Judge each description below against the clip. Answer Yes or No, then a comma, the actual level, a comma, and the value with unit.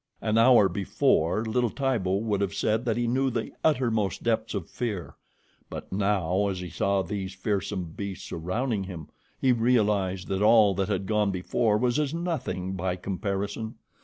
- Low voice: Yes, low, 105 Hz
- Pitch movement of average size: Yes, average, 3.4 semitones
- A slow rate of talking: No, average, 165 wpm